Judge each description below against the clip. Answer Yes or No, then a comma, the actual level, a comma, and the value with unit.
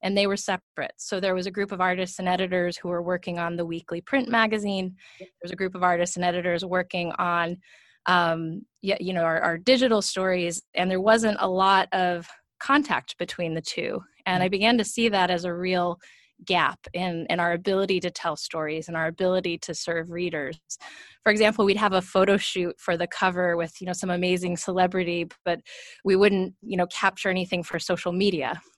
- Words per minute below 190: No, average, 200 wpm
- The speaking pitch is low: No, medium, 180 Hz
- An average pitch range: No, narrow, 2.0 semitones